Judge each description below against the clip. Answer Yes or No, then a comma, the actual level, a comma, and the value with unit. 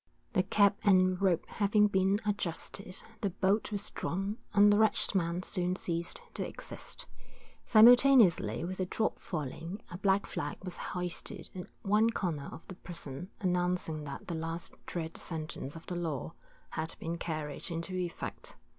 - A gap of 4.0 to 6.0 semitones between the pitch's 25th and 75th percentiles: No, average, 3.3 semitones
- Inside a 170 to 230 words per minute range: No, average, 155 wpm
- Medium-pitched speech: Yes, medium, 180 Hz